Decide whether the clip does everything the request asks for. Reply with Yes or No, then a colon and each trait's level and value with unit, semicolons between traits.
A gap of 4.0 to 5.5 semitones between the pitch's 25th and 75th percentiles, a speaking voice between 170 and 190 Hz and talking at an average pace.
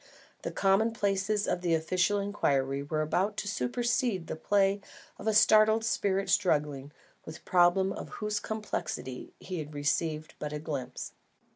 Yes: average, 5.1 semitones; medium, 185 Hz; average, 150 wpm